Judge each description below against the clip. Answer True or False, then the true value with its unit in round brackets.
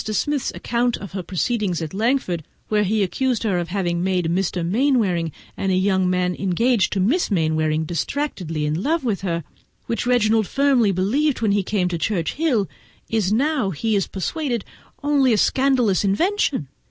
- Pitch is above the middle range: True (205 Hz)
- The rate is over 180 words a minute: False (165 wpm)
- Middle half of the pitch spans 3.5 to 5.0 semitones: False (5.5 semitones)